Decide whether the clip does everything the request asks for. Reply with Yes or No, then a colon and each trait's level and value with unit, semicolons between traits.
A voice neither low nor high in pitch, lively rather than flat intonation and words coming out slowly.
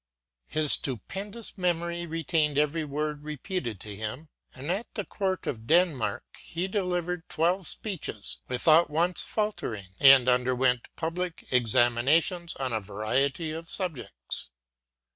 Yes: medium, 155 Hz; wide, 5.8 semitones; slow, 125 wpm